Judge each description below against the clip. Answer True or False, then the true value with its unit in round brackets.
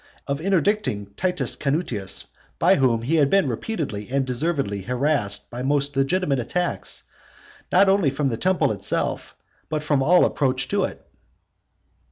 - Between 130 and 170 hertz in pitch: True (140 Hz)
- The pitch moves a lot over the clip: True (5.9 semitones)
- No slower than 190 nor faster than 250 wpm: False (145 wpm)